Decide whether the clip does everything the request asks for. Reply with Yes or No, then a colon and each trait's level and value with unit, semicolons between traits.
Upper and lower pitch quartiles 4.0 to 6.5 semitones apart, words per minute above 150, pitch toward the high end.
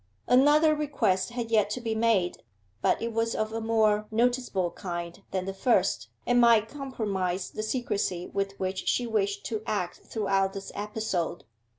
No: average, 3.2 semitones; average, 165 wpm; high, 215 Hz